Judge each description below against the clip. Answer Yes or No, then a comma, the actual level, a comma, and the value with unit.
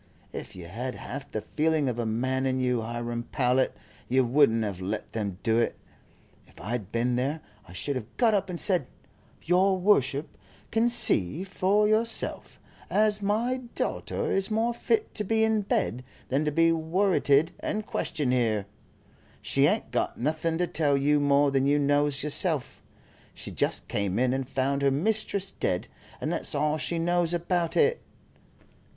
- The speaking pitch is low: No, medium, 145 Hz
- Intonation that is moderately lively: No, wide, 6.9 semitones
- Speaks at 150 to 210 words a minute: Yes, average, 170 wpm